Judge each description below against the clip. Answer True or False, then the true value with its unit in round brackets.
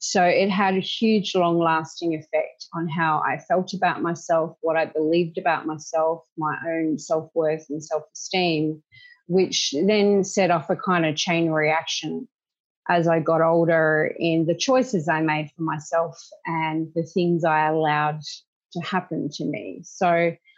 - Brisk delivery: False (165 wpm)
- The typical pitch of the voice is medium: True (165 Hz)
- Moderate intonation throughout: False (2.3 semitones)